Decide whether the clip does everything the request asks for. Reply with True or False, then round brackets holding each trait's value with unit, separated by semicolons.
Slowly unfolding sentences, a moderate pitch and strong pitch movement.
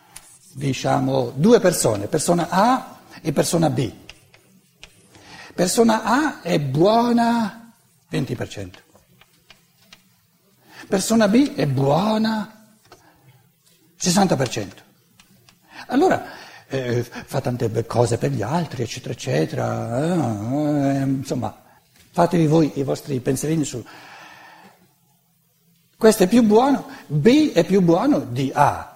True (95 wpm; 160 Hz; 8.1 semitones)